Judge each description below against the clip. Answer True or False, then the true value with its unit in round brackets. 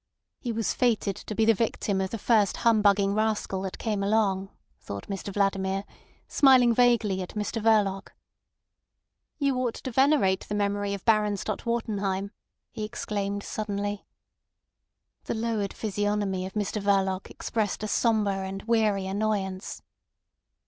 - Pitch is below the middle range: False (205 Hz)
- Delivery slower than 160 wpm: True (140 wpm)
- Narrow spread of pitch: True (2.2 semitones)